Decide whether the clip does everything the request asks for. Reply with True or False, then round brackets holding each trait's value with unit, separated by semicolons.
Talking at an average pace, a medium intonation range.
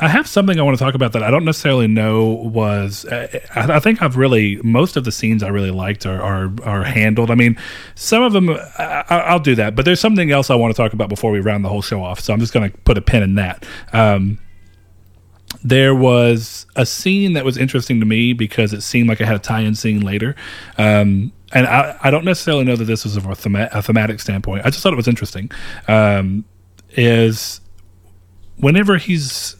False (225 wpm; 4.6 semitones)